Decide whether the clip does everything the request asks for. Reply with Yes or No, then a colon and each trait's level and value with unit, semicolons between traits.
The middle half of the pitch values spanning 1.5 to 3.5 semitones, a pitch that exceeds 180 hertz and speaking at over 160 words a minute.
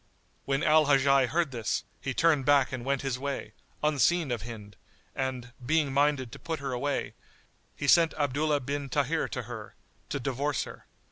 No: narrow, 2.5 semitones; medium, 140 Hz; average, 180 wpm